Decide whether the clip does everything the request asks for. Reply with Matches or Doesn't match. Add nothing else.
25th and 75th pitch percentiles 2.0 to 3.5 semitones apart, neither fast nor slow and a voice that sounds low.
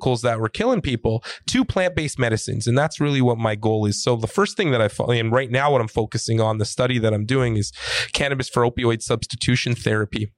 Doesn't match